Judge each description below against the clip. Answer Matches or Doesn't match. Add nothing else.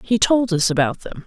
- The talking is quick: Matches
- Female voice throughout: Matches